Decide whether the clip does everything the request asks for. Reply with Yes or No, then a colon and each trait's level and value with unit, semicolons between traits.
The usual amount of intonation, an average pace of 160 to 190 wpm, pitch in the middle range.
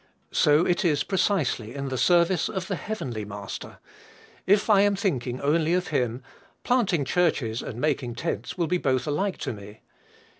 No: wide, 7.1 semitones; average, 165 wpm; medium, 155 Hz